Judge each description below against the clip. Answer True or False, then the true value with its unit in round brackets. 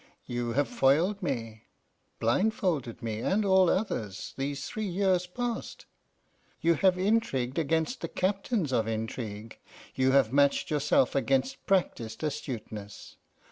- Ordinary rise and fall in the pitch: False (7.8 semitones)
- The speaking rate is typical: False (125 wpm)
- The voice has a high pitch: False (140 Hz)